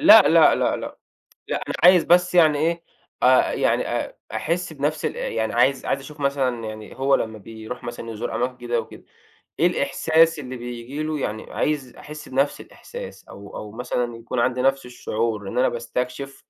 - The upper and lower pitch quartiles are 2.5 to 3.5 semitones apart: No, average, 4.3 semitones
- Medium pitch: No, low, 130 Hz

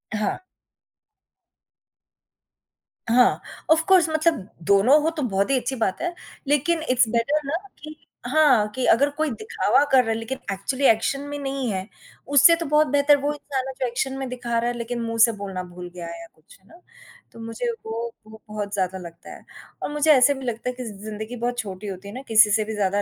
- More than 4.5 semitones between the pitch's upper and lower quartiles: Yes, average, 5.2 semitones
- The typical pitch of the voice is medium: No, high, 240 Hz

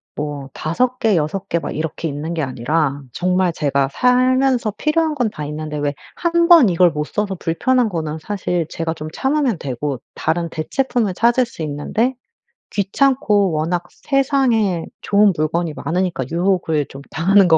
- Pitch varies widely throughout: Yes, wide, 7.4 semitones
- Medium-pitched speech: Yes, medium, 175 Hz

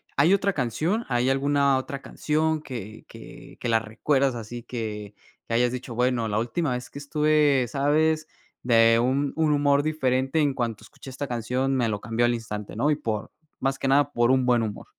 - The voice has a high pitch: No, low, 130 Hz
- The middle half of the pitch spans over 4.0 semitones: No, average, 3.7 semitones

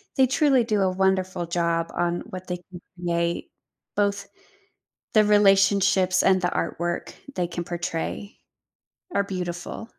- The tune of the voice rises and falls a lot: No, narrow, 2.5 semitones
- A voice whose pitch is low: No, medium, 185 Hz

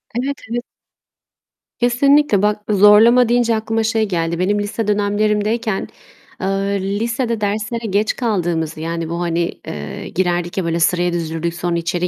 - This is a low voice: No, high, 205 Hz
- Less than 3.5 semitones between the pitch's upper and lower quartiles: No, average, 4.6 semitones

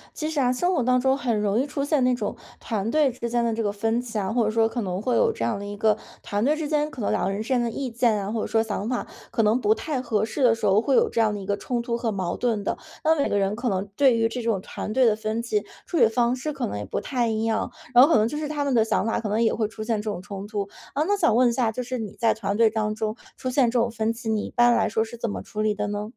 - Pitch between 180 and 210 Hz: No, high, 230 Hz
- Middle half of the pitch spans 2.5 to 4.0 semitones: Yes, average, 2.9 semitones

